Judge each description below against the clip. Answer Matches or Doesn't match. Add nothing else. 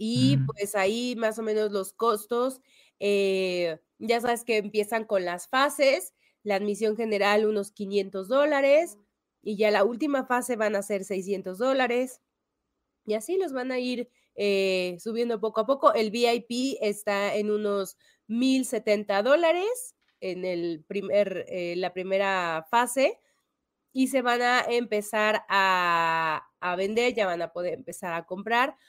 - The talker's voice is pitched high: Matches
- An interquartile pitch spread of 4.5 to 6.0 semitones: Doesn't match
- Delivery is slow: Doesn't match